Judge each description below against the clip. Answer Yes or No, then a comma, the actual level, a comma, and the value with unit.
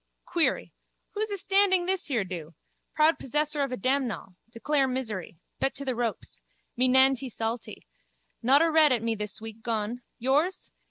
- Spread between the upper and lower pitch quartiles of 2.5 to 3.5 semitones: No, average, 5.1 semitones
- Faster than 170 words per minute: No, average, 155 wpm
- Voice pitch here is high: Yes, very high, 260 Hz